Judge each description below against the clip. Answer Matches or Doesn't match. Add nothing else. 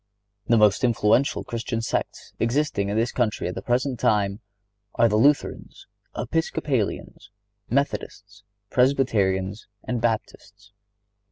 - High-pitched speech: Doesn't match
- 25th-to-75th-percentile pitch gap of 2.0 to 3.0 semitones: Doesn't match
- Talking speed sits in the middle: Doesn't match